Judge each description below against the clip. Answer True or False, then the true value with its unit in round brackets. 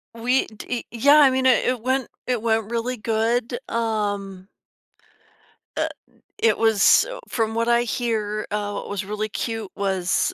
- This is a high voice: True (225 Hz)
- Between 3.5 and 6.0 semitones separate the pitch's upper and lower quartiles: False (2.6 semitones)